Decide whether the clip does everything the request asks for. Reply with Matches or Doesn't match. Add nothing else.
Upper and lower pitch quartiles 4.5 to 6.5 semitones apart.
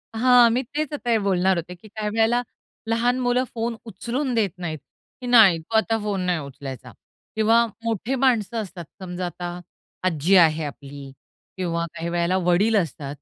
Matches